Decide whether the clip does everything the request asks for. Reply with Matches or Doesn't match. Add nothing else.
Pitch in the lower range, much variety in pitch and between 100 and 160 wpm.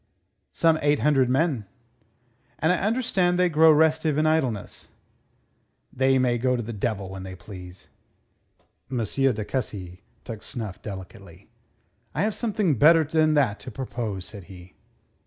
Matches